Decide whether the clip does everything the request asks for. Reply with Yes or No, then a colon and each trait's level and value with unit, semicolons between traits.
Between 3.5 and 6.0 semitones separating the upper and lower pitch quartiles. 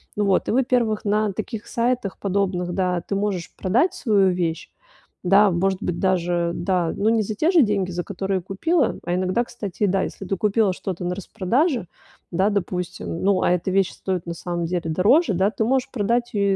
No: average, 3.1 semitones